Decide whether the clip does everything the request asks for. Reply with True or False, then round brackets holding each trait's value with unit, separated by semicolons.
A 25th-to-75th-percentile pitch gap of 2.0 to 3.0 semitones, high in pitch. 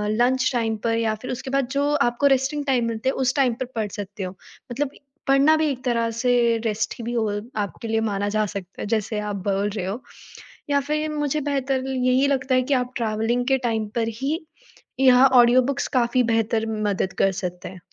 False (3.6 semitones; 240 Hz)